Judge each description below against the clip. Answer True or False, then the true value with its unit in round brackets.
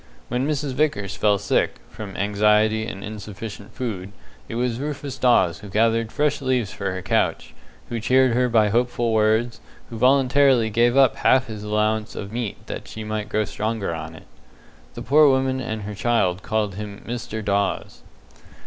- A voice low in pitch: True (110 Hz)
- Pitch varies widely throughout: False (3.2 semitones)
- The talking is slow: False (175 wpm)